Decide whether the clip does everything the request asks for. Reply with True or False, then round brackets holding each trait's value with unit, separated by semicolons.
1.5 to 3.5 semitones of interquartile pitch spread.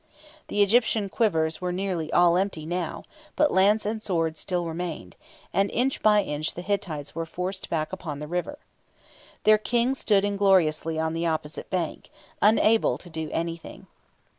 False (4.0 semitones)